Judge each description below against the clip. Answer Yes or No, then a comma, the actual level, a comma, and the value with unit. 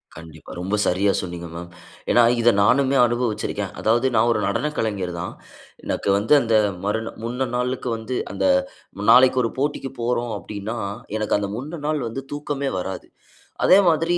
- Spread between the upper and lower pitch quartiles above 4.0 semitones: Yes, average, 4.6 semitones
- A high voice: No, low, 115 Hz